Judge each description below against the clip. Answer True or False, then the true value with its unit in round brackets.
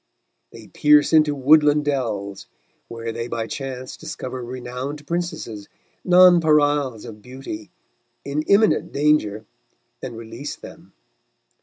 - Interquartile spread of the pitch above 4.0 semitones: True (4.4 semitones)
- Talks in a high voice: False (135 Hz)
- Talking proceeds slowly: True (110 wpm)